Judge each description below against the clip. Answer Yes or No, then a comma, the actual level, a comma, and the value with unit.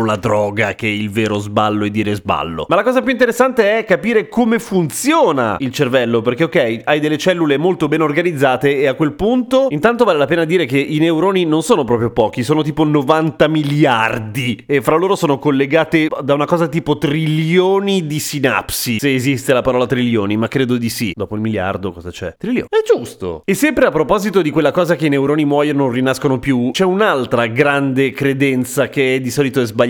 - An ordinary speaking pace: No, fast, 205 wpm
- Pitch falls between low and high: Yes, medium, 145 Hz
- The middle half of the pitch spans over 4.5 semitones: Yes, average, 5.2 semitones